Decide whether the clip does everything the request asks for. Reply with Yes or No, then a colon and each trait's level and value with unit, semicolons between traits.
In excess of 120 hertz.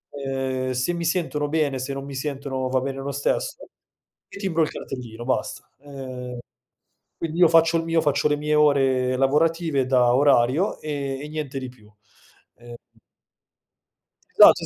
Yes: medium, 140 Hz